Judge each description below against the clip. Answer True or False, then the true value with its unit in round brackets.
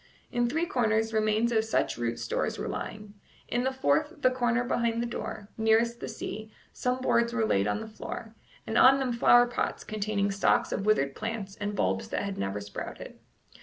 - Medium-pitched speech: False (220 Hz)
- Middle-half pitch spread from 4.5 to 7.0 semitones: False (3.0 semitones)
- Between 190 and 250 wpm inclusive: True (195 wpm)